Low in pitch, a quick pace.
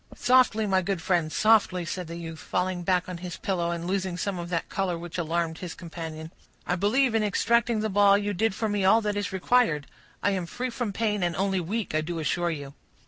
No: medium, 185 Hz; fast, 225 wpm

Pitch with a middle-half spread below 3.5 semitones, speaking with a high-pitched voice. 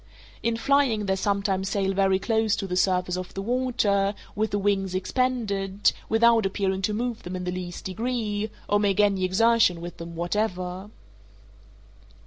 Yes: average, 2.9 semitones; high, 200 Hz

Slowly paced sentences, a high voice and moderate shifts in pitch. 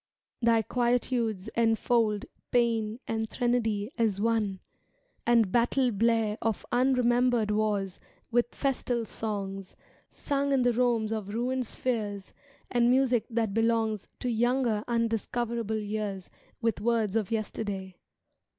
No: slow, 115 wpm; high, 225 Hz; narrow, 2.3 semitones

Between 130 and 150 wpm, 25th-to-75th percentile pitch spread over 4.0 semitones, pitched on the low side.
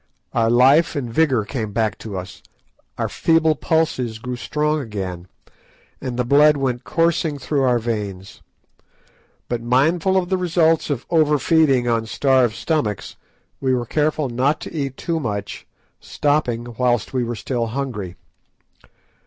Yes: average, 145 wpm; average, 4.7 semitones; low, 130 Hz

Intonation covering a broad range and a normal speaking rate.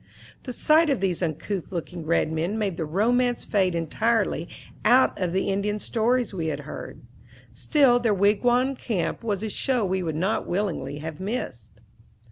Yes: wide, 5.9 semitones; average, 165 wpm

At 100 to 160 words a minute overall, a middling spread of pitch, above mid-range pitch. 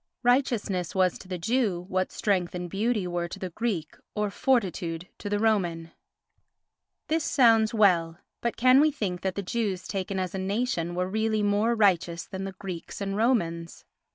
No: average, 175 wpm; average, 3.8 semitones; high, 195 Hz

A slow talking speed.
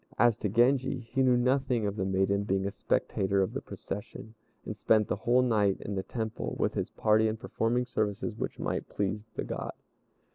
No: average, 195 wpm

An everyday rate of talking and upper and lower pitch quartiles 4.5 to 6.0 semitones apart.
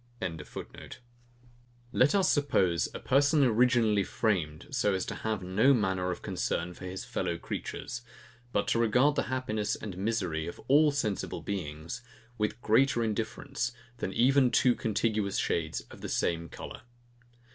Yes: average, 145 wpm; average, 5.3 semitones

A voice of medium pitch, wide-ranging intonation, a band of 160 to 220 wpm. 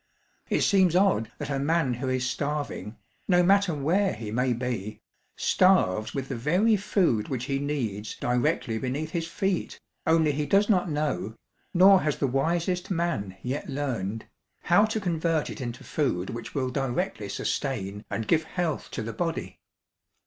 Yes: medium, 145 Hz; wide, 6.3 semitones; average, 165 wpm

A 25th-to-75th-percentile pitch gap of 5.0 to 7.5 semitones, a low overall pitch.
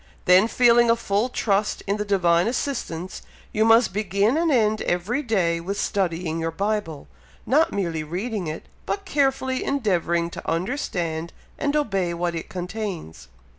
No: average, 5.3 semitones; high, 200 Hz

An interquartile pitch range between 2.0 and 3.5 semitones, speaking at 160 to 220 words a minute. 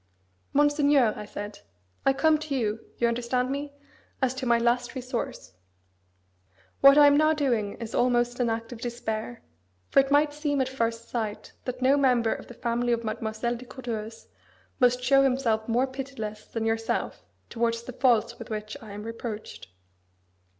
Yes: average, 3.0 semitones; average, 170 wpm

